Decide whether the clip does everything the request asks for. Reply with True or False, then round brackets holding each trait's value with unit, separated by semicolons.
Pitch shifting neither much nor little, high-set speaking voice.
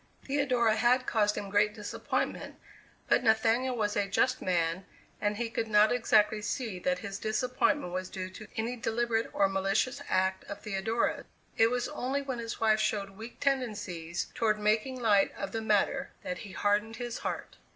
True (3.2 semitones; 215 Hz)